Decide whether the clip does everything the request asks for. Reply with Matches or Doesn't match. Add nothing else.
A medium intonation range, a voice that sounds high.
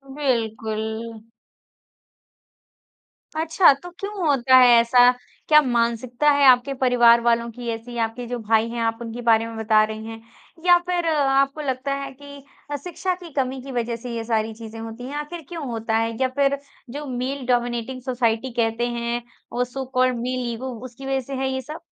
Matches